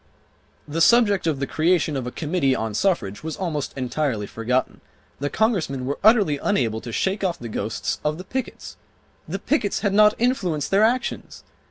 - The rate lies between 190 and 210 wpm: No, average, 175 wpm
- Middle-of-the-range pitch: Yes, medium, 160 Hz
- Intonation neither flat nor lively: No, wide, 7.5 semitones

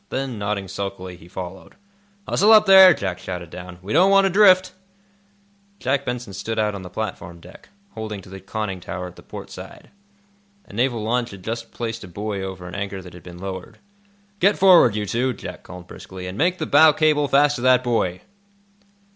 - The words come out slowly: No, average, 200 wpm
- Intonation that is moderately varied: No, wide, 6.6 semitones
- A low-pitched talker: Yes, low, 105 Hz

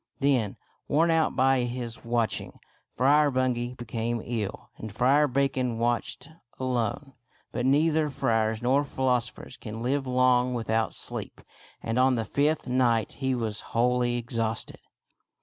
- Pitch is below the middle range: Yes, low, 125 Hz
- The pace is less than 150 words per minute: Yes, average, 140 wpm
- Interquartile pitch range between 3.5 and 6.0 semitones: No, narrow, 2.4 semitones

